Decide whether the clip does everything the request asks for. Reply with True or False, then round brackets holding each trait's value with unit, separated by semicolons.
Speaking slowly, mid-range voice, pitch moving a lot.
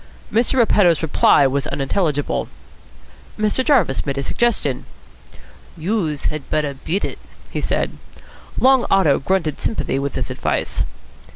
True (125 wpm; 160 Hz; 7.2 semitones)